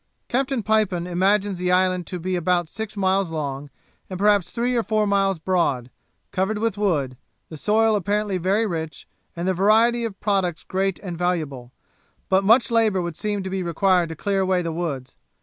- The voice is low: No, high, 190 Hz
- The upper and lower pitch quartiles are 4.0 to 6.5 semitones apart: No, average, 3.2 semitones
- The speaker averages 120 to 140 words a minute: No, average, 185 wpm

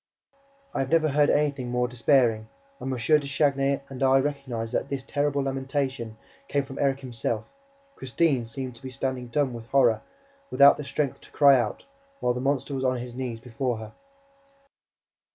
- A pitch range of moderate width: No, narrow, 2.2 semitones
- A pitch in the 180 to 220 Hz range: No, low, 135 Hz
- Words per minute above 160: Yes, average, 175 wpm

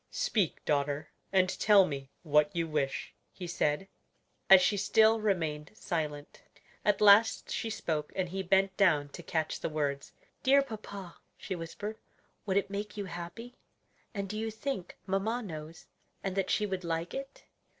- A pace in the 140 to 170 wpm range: Yes, average, 160 wpm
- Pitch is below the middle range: No, high, 190 Hz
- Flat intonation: No, average, 4.8 semitones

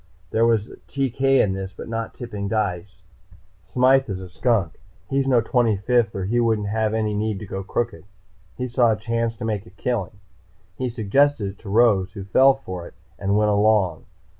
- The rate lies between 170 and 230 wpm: Yes, average, 190 wpm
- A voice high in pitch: No, low, 110 Hz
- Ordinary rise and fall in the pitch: Yes, average, 3.4 semitones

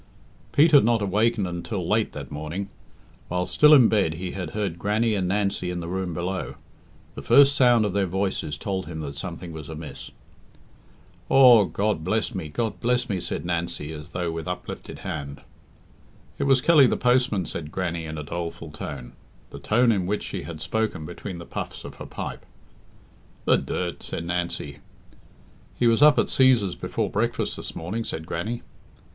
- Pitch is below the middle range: Yes, very low, 95 Hz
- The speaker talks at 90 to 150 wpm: No, average, 180 wpm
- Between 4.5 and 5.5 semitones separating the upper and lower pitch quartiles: Yes, average, 5.2 semitones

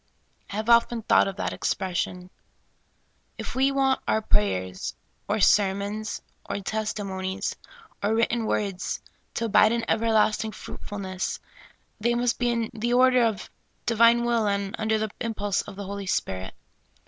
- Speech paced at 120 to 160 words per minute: Yes, average, 155 wpm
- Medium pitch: No, high, 215 Hz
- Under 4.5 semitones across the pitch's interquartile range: Yes, average, 2.9 semitones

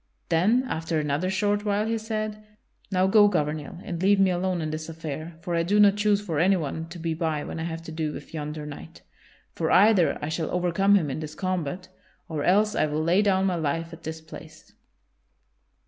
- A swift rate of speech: Yes, fast, 210 wpm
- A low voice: No, medium, 170 Hz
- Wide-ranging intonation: No, average, 3.8 semitones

